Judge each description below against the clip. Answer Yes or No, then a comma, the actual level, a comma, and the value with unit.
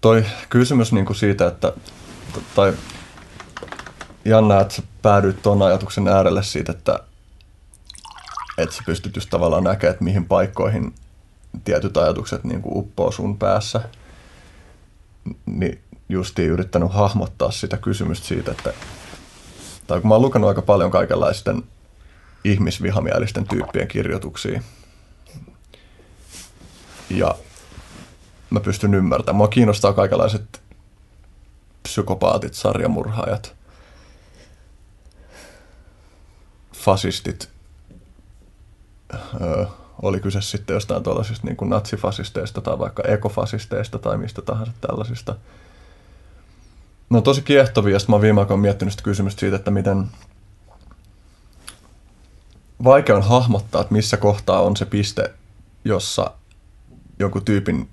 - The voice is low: Yes, low, 100 Hz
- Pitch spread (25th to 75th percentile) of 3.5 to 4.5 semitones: No, average, 3.1 semitones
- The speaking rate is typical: Yes, average, 105 wpm